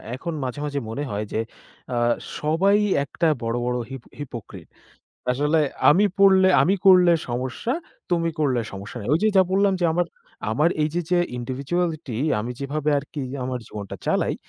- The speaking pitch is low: No, medium, 145 Hz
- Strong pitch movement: Yes, wide, 5.7 semitones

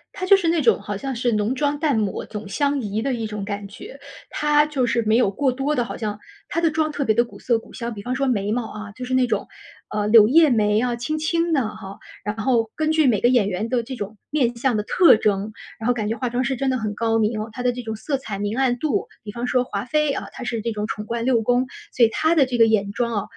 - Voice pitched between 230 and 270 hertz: Yes, high, 240 Hz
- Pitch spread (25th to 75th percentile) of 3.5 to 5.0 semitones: Yes, average, 3.9 semitones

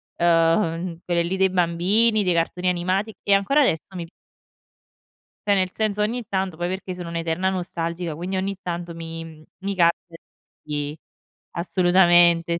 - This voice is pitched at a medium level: Yes, medium, 175 Hz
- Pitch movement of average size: No, narrow, 2.2 semitones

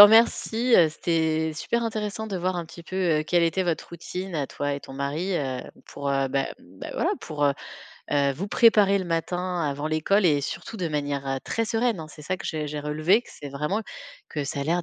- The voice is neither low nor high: Yes, medium, 165 Hz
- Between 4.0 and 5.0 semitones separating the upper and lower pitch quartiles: Yes, average, 4.7 semitones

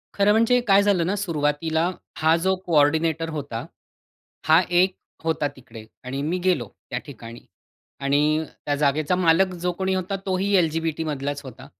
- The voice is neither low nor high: Yes, medium, 160 Hz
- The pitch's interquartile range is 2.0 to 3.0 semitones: No, average, 4.1 semitones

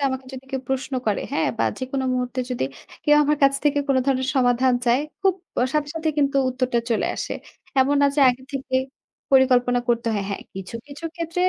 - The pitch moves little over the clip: Yes, narrow, 2.3 semitones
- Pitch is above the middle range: Yes, very high, 260 Hz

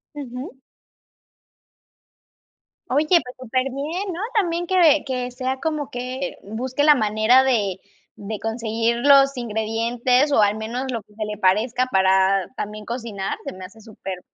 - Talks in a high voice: Yes, high, 245 Hz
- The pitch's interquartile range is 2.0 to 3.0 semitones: No, average, 4.1 semitones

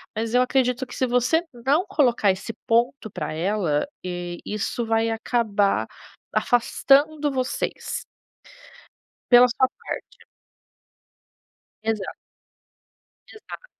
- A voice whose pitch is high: Yes, high, 240 Hz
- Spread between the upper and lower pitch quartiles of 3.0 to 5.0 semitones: Yes, average, 3.8 semitones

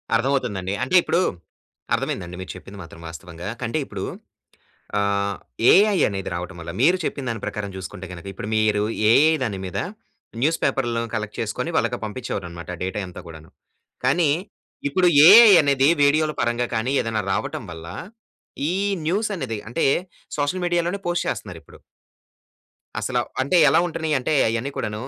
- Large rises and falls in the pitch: Yes, wide, 7.3 semitones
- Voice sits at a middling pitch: No, low, 115 Hz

